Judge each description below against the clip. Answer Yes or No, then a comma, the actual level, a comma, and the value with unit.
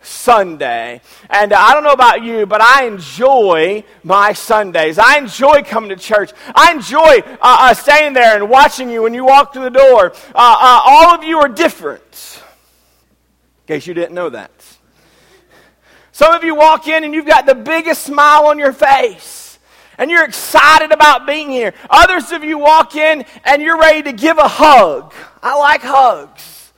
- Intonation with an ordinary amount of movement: No, wide, 6.2 semitones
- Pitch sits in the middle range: No, very high, 285 Hz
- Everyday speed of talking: Yes, average, 180 wpm